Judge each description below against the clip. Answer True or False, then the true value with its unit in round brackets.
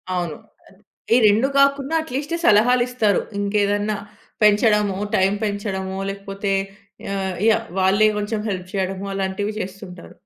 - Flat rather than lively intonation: True (2.2 semitones)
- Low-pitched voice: False (205 Hz)